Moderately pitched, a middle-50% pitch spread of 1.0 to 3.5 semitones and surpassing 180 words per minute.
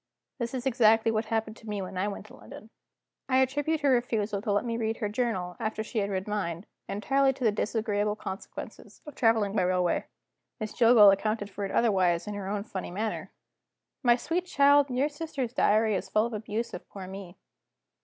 No: high, 215 Hz; average, 3.1 semitones; average, 200 wpm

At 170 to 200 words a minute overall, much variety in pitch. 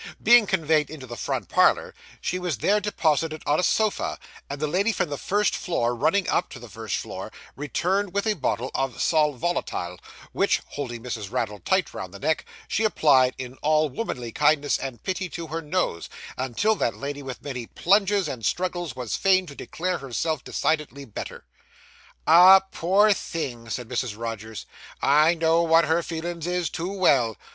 Yes: average, 175 wpm; wide, 6.0 semitones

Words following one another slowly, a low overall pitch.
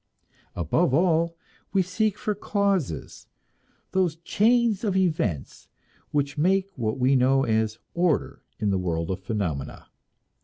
No: slow, 125 wpm; medium, 155 Hz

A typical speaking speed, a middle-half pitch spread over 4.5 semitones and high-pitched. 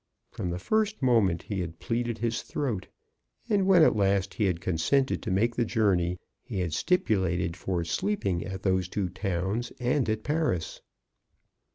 No: average, 165 wpm; average, 5.2 semitones; low, 100 Hz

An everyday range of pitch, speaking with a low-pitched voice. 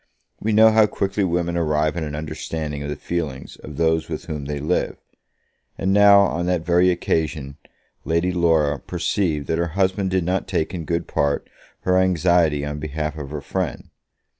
Yes: average, 3.3 semitones; very low, 85 Hz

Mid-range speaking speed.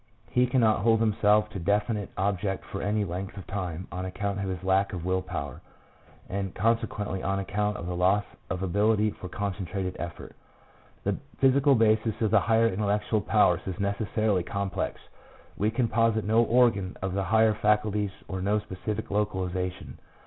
Yes: average, 170 wpm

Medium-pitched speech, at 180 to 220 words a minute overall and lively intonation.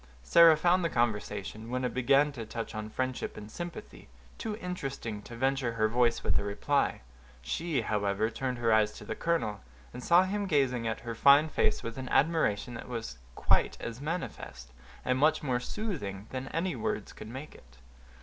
No: low, 125 Hz; average, 185 wpm; wide, 5.9 semitones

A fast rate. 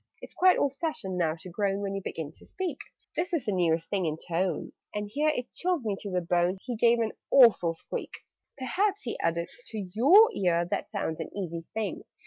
Yes: fast, 215 wpm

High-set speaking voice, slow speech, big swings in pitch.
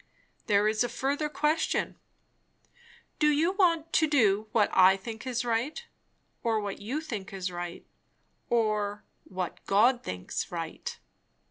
Yes: high, 225 Hz; slow, 125 wpm; wide, 6.7 semitones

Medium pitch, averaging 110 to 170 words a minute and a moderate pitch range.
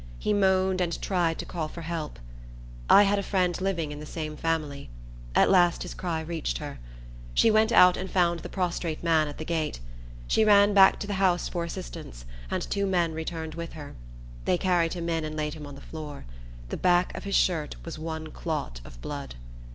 No: medium, 170 Hz; fast, 205 wpm; average, 3.0 semitones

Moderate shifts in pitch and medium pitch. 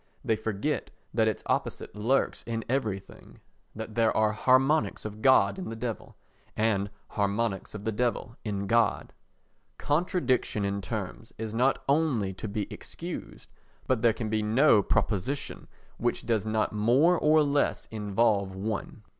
No: average, 3.6 semitones; low, 110 Hz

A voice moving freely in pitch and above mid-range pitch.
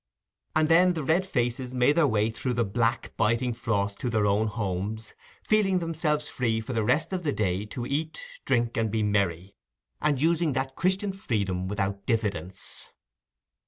No: wide, 6.6 semitones; low, 120 Hz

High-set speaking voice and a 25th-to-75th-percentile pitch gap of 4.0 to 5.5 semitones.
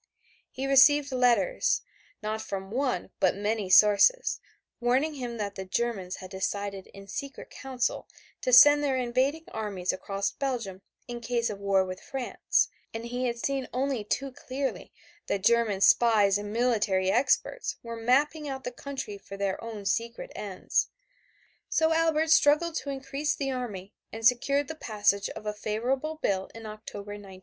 Yes: high, 235 Hz; average, 5.1 semitones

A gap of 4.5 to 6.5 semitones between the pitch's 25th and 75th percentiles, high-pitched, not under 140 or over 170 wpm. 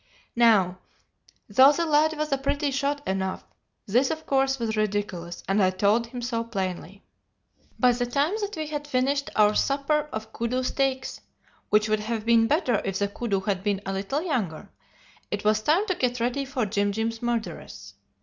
No: average, 5.2 semitones; high, 235 Hz; average, 180 wpm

